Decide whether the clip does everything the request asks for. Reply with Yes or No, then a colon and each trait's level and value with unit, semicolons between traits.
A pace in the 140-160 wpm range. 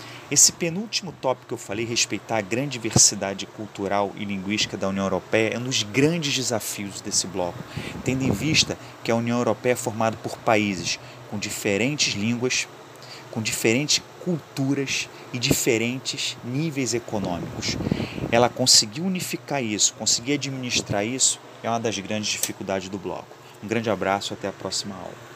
Yes: average, 155 wpm